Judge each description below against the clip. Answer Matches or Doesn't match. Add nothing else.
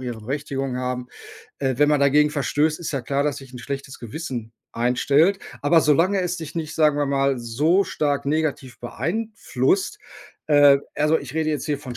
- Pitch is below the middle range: Doesn't match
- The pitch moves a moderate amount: Matches